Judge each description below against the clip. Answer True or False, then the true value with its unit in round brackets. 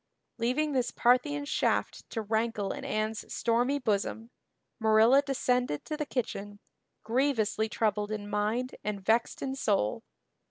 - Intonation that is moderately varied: True (3.2 semitones)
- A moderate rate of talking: False (130 wpm)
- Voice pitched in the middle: False (230 Hz)